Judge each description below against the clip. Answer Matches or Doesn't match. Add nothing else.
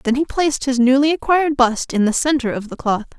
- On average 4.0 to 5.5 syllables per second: Doesn't match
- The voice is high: Matches